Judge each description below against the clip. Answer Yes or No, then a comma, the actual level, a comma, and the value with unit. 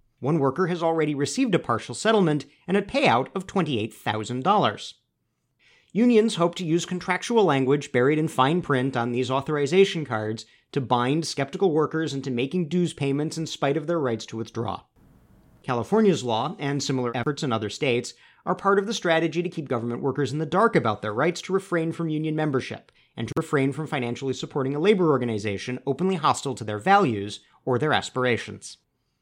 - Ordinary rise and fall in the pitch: No, wide, 5.7 semitones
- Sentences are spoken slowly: No, average, 180 wpm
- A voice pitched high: No, medium, 145 Hz